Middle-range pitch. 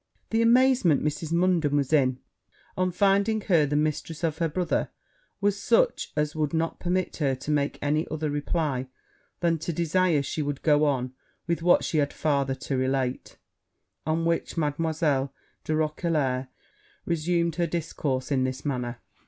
Yes: medium, 155 Hz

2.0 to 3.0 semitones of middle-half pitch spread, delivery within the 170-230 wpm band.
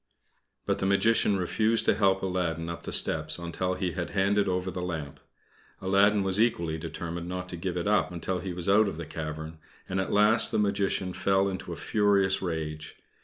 Yes: narrow, 2.6 semitones; average, 195 wpm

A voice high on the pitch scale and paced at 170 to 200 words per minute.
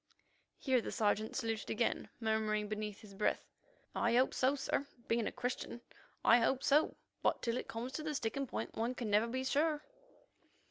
Yes: high, 235 Hz; average, 180 wpm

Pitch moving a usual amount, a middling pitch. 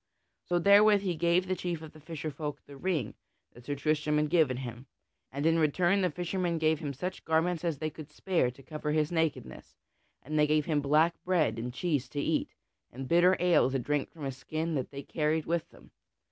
Yes: average, 3.2 semitones; medium, 155 Hz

